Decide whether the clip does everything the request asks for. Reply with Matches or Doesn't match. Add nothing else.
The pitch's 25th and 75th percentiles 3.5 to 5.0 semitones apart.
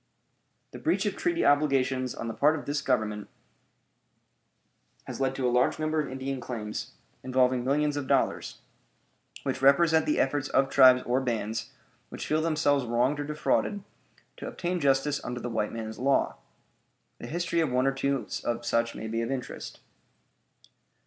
Doesn't match